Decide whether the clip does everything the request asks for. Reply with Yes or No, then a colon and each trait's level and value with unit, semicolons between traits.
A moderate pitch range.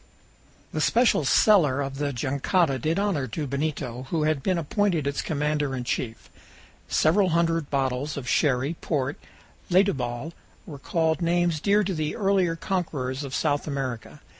Yes: average, 4.0 semitones